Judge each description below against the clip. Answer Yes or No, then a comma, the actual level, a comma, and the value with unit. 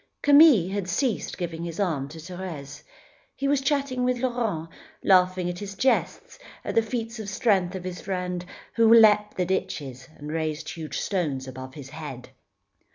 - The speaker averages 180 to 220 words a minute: No, average, 165 wpm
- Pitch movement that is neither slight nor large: No, wide, 6.1 semitones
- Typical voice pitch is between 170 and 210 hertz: Yes, medium, 185 Hz